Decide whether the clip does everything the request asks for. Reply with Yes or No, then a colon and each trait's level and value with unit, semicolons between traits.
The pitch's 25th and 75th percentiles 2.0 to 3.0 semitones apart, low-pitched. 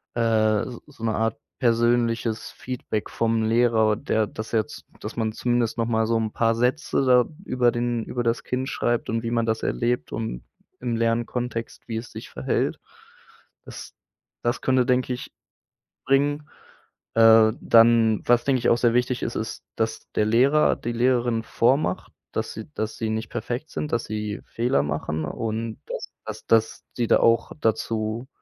No: narrow, 1.6 semitones; low, 115 Hz